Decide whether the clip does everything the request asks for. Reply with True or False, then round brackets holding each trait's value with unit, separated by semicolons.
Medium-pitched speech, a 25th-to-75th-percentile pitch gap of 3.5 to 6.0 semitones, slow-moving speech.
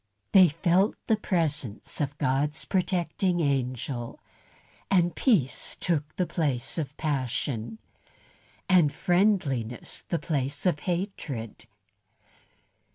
True (150 Hz; 5.2 semitones; 95 wpm)